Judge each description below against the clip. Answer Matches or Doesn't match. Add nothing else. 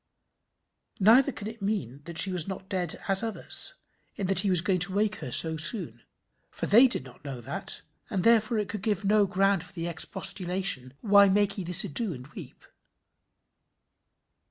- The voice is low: Doesn't match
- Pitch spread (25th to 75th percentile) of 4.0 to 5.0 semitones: Doesn't match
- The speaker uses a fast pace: Doesn't match